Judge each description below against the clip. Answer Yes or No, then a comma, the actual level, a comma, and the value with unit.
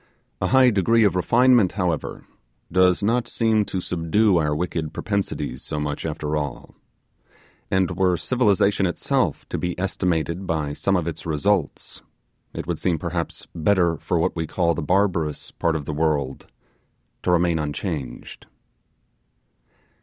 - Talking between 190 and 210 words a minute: No, average, 145 wpm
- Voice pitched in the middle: No, very low, 85 Hz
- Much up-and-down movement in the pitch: No, average, 3.8 semitones